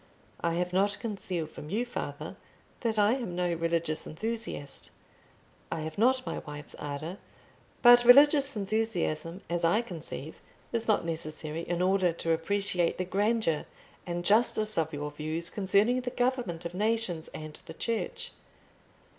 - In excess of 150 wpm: No, average, 145 wpm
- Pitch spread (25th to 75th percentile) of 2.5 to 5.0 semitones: No, wide, 5.4 semitones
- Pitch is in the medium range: Yes, medium, 180 Hz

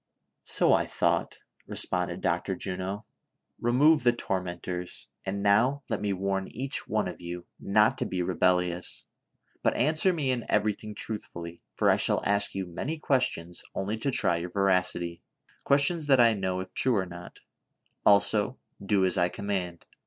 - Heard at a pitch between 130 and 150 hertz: No, low, 100 Hz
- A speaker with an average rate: Yes, average, 160 wpm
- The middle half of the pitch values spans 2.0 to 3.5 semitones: No, average, 4.8 semitones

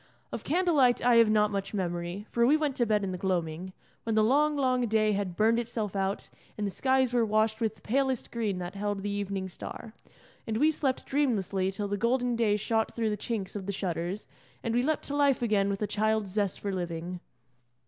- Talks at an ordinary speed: No, fast, 220 wpm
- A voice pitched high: Yes, high, 215 Hz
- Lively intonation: No, average, 3.6 semitones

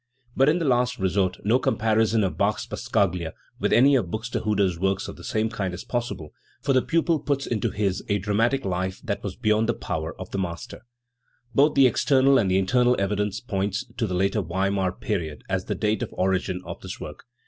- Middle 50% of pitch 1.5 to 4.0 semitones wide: No, average, 4.5 semitones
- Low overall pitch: Yes, low, 105 Hz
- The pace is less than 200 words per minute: No, fast, 205 wpm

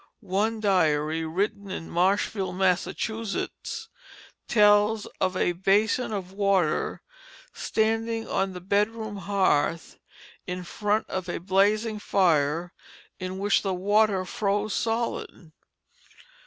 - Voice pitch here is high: Yes, high, 195 Hz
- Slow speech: Yes, slow, 105 wpm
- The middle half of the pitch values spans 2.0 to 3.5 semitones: Yes, average, 2.7 semitones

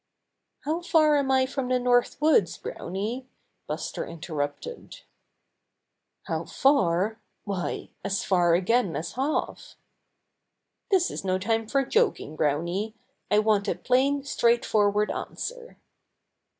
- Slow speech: Yes, slow, 115 wpm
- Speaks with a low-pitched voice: No, high, 225 Hz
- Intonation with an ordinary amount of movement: No, wide, 6.4 semitones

